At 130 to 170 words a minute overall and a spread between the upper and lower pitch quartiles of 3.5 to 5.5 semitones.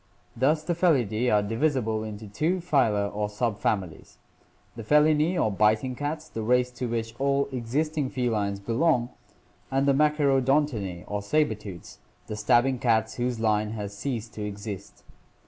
Yes: average, 150 wpm; average, 4.9 semitones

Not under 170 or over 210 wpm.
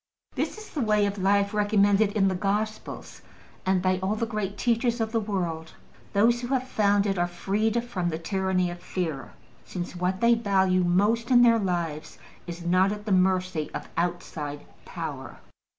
Yes: average, 180 wpm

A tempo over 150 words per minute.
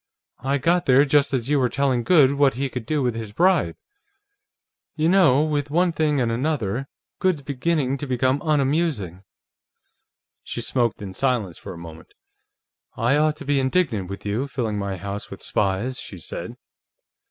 Yes: average, 170 wpm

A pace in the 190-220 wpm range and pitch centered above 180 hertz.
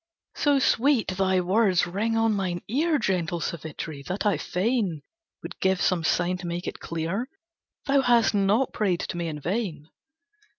No: average, 165 wpm; high, 190 Hz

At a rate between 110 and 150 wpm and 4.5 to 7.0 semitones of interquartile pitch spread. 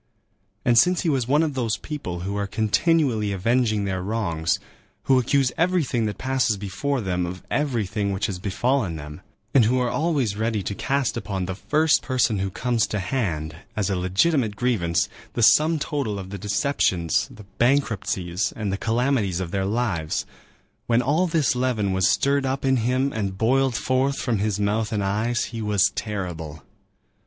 No: average, 175 wpm; average, 5.3 semitones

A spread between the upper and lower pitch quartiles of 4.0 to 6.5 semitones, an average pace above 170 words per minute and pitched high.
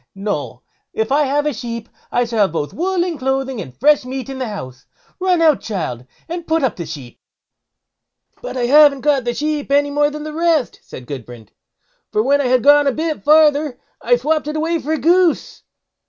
Yes: average, 5.3 semitones; fast, 205 wpm; very high, 275 Hz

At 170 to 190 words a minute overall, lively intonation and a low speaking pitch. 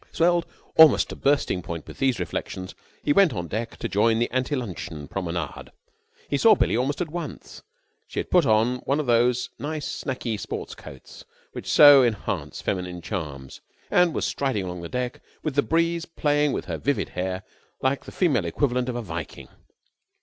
Yes: average, 180 wpm; wide, 7.6 semitones; low, 125 Hz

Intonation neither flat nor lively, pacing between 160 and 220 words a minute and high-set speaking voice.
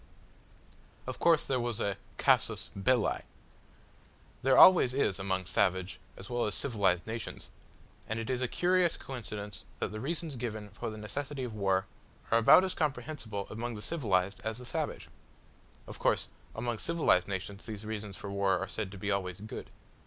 No: average, 4.3 semitones; average, 170 wpm; low, 110 Hz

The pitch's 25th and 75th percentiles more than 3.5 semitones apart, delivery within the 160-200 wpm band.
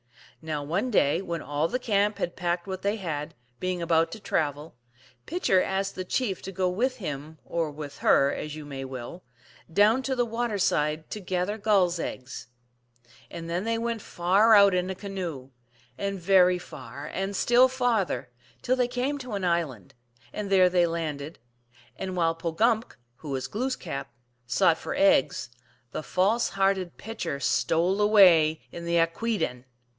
Yes: average, 4.7 semitones; average, 170 wpm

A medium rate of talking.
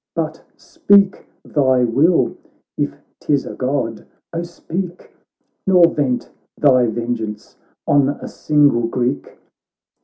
No: slow, 110 wpm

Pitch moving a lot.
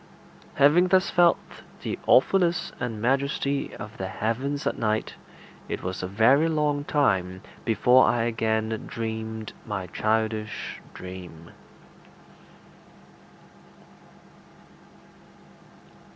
No: average, 4.9 semitones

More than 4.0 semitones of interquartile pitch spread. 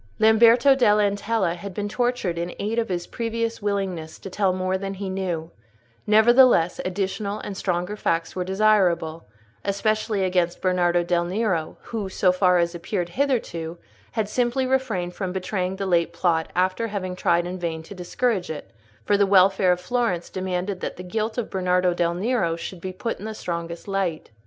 No: average, 3.3 semitones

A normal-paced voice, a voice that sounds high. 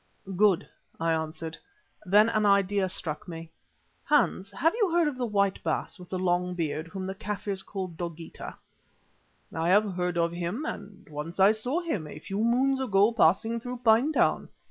Yes: average, 170 wpm; high, 195 Hz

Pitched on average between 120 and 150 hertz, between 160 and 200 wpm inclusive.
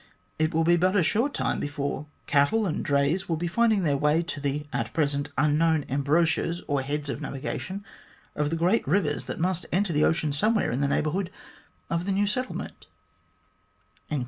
No: medium, 160 Hz; average, 185 wpm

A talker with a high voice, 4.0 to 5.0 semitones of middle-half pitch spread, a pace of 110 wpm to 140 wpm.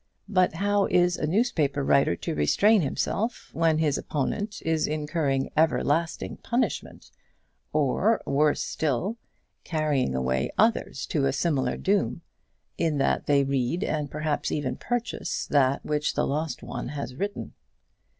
No: medium, 155 Hz; average, 4.6 semitones; slow, 135 wpm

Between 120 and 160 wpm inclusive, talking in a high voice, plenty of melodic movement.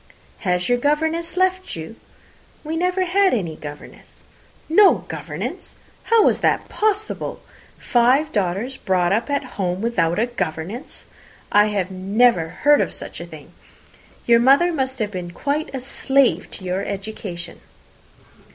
Yes: average, 140 wpm; high, 240 Hz; wide, 8.3 semitones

